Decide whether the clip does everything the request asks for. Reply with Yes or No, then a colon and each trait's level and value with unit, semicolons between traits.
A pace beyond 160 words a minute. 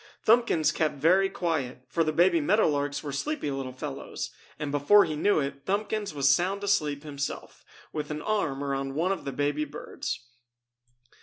Yes: average, 170 wpm